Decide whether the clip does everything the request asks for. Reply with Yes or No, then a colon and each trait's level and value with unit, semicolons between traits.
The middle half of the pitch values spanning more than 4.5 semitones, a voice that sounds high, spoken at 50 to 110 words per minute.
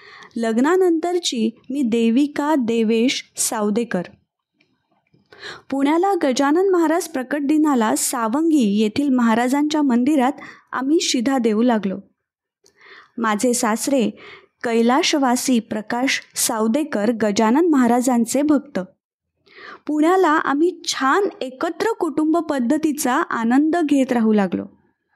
Yes: average, 5.1 semitones; very high, 275 Hz; average, 85 wpm